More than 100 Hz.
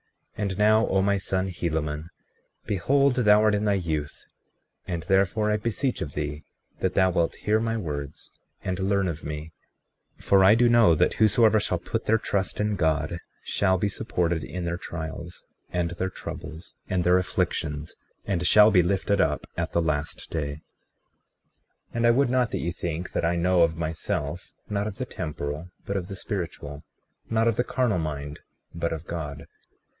No: very low, 90 Hz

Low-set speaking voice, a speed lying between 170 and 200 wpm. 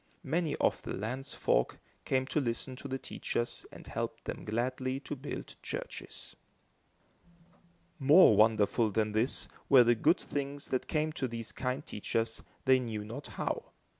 No: low, 130 Hz; average, 155 wpm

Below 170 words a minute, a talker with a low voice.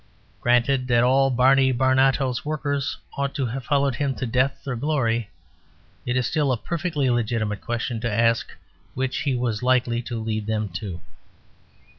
Yes: average, 160 wpm; low, 125 Hz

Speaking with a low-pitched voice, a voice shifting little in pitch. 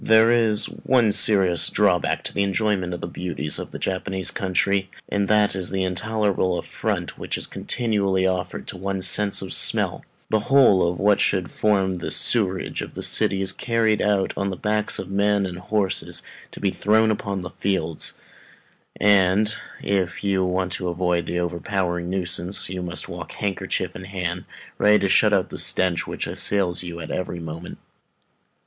Yes: very low, 95 Hz; narrow, 2.3 semitones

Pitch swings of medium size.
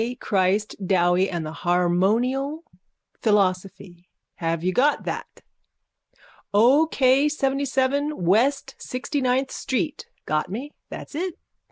No: wide, 7.1 semitones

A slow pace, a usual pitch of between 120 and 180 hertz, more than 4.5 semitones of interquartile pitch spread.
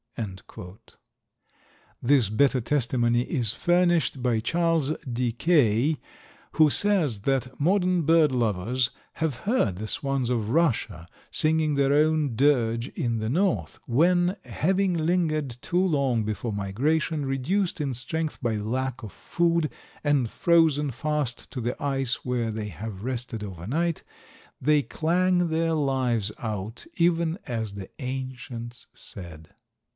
Yes: slow, 130 wpm; low, 135 Hz; wide, 5.5 semitones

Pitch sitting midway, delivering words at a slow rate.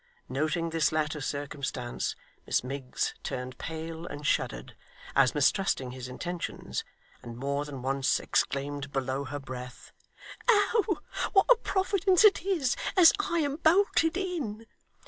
Yes: medium, 155 Hz; slow, 130 wpm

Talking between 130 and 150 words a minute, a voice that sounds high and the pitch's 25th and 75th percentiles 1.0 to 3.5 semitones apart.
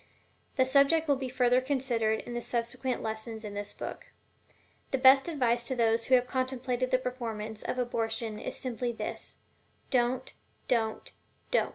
Yes: average, 140 wpm; high, 245 Hz; narrow, 2.4 semitones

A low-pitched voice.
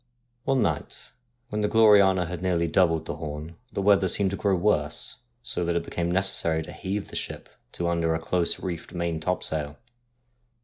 Yes: very low, 85 Hz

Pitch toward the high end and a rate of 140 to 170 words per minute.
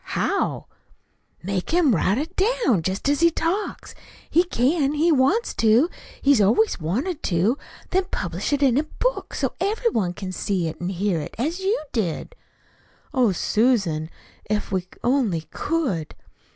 Yes: high, 245 Hz; average, 150 wpm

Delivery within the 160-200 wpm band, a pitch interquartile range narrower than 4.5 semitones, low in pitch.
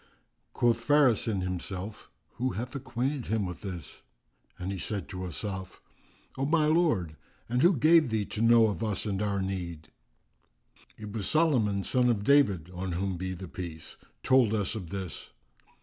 No: average, 165 wpm; average, 5.0 semitones; low, 105 Hz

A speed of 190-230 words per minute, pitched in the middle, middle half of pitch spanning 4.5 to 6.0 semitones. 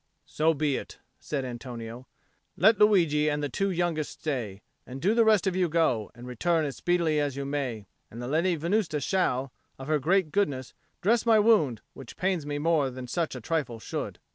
Yes: average, 195 wpm; medium, 150 Hz; wide, 5.4 semitones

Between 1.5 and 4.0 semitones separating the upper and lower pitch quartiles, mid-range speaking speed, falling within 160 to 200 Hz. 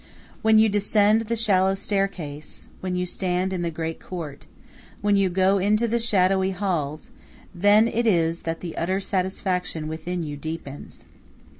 Yes: average, 3.5 semitones; average, 155 wpm; medium, 185 Hz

